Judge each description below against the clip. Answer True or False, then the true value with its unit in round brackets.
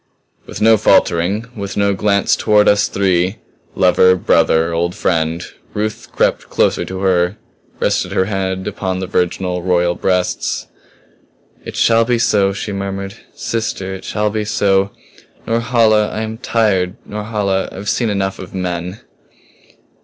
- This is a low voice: True (95 Hz)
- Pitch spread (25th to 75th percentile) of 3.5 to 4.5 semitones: False (2.4 semitones)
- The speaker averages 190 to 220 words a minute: False (145 wpm)